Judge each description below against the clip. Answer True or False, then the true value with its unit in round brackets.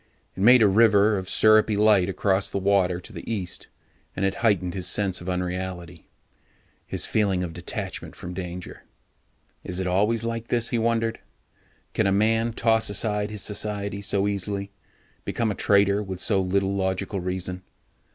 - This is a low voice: True (100 Hz)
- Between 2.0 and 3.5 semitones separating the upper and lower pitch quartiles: True (2.6 semitones)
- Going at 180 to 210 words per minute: False (165 wpm)